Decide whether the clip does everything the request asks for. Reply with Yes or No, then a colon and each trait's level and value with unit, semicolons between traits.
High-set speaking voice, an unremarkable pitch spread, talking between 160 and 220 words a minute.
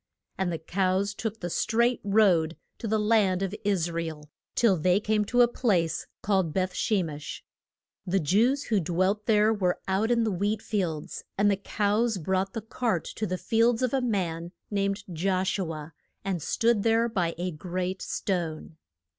Yes: high, 195 Hz; average, 3.7 semitones; average, 180 wpm